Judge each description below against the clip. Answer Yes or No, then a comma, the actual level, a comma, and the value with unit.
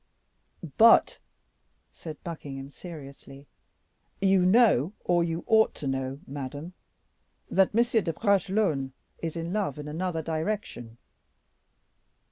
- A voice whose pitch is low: No, medium, 165 Hz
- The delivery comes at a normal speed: No, slow, 105 wpm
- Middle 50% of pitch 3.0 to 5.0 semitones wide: No, wide, 5.5 semitones